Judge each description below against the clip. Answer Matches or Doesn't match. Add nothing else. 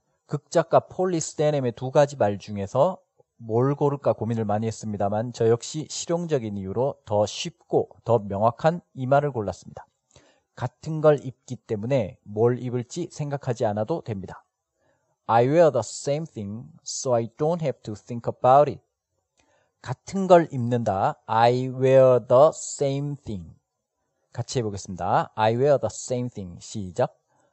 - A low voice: Matches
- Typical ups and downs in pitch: Matches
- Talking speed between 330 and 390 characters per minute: Matches